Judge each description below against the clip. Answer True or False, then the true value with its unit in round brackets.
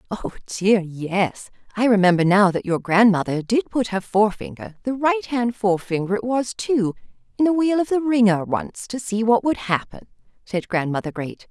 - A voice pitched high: True (210 Hz)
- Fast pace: False (175 wpm)